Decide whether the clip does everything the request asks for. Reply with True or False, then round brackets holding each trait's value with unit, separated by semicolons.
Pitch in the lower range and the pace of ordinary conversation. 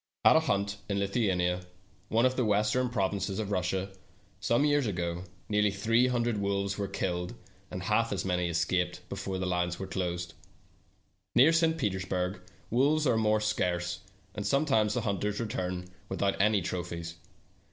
True (100 Hz; 160 wpm)